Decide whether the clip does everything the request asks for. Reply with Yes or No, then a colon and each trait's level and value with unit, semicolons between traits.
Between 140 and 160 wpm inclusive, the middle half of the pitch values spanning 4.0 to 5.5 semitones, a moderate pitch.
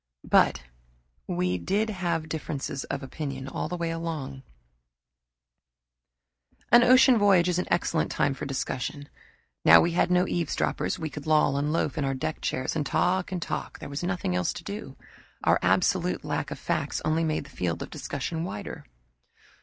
No: average, 170 wpm; average, 4.4 semitones; medium, 155 Hz